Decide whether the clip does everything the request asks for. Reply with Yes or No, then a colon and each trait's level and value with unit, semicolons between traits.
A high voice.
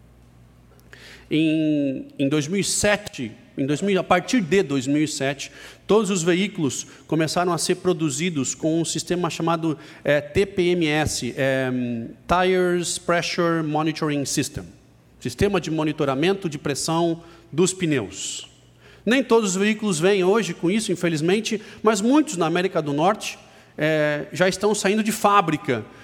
No: medium, 165 Hz